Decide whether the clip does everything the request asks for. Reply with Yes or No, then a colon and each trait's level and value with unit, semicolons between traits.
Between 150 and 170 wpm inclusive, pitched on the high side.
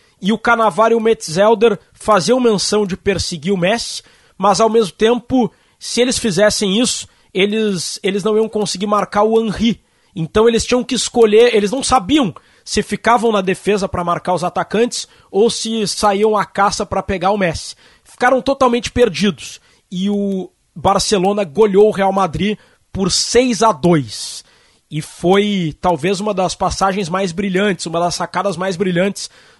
Yes: average, 160 wpm; high, 205 Hz